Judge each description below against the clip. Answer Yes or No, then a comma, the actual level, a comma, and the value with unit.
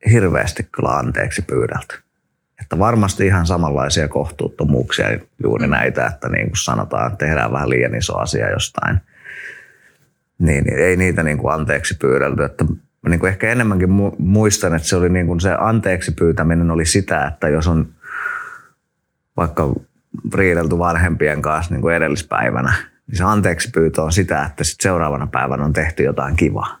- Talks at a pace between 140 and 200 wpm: Yes, average, 150 wpm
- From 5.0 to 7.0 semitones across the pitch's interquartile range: No, average, 3.4 semitones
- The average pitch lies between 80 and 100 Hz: Yes, very low, 85 Hz